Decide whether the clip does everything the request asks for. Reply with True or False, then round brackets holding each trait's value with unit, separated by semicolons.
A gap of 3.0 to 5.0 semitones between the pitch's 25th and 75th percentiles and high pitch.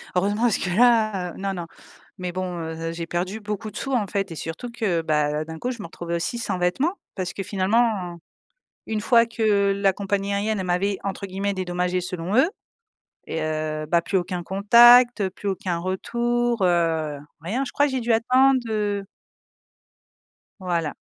True (4.1 semitones; 195 Hz)